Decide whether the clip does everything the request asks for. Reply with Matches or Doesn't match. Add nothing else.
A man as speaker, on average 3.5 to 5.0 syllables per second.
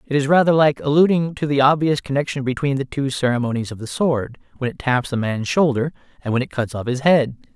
Doesn't match